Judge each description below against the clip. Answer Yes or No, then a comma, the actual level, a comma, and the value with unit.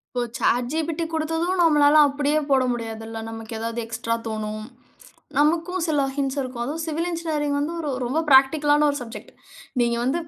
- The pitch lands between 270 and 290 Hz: Yes, very high, 285 Hz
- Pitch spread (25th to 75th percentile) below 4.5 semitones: No, average, 4.9 semitones